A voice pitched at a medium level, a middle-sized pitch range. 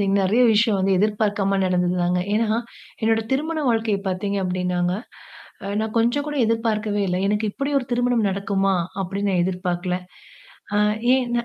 No: high, 205 Hz; average, 3.3 semitones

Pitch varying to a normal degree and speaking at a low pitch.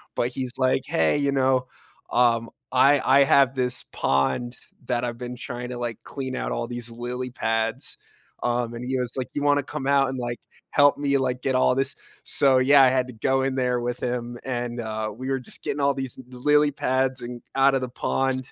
No: narrow, 1.8 semitones; low, 125 Hz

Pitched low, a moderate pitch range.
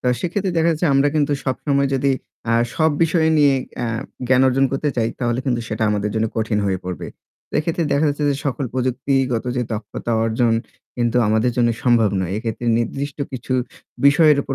Yes: low, 130 Hz; average, 3.8 semitones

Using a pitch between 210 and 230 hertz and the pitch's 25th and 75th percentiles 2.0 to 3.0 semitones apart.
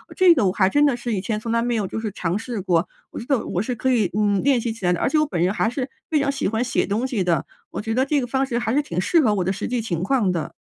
No: high, 225 Hz; average, 5.2 semitones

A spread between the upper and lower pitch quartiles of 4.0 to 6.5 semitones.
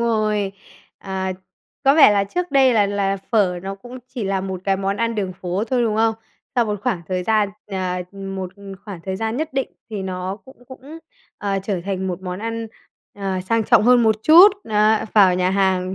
No: average, 3.2 semitones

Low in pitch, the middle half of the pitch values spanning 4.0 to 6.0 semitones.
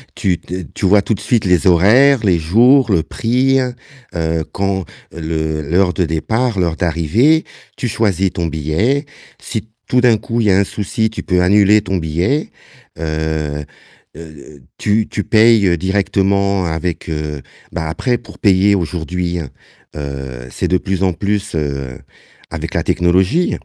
Yes: very low, 95 Hz; average, 4.8 semitones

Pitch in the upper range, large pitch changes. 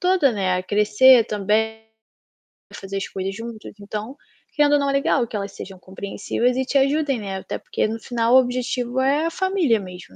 No: high, 230 Hz; average, 4.9 semitones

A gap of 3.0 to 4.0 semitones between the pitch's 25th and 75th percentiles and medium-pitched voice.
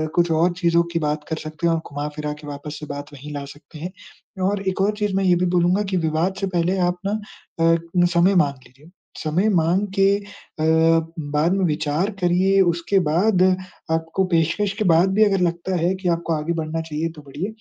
Yes: average, 3.4 semitones; medium, 170 Hz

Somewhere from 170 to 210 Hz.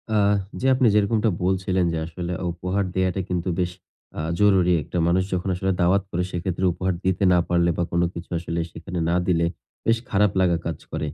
No: very low, 90 Hz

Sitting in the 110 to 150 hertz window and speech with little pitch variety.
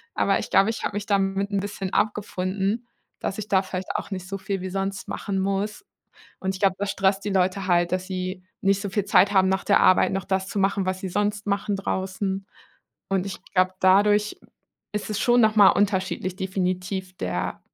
No: high, 195 Hz; narrow, 1.3 semitones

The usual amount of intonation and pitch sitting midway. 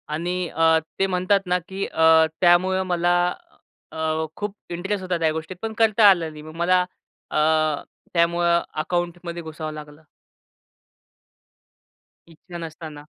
No: narrow, 2.3 semitones; medium, 170 Hz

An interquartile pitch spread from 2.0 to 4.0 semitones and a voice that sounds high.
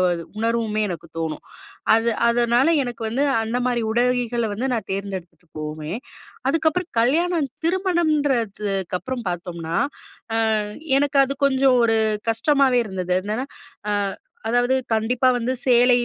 No: average, 4.6 semitones; high, 235 Hz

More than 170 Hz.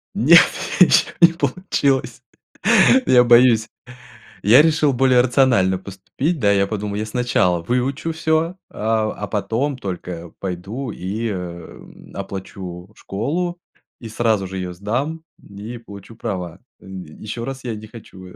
No: low, 110 Hz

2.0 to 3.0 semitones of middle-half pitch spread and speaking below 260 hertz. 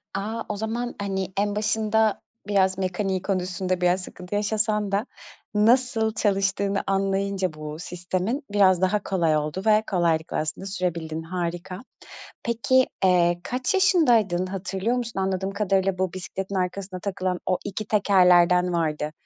Yes: narrow, 2.6 semitones; high, 190 Hz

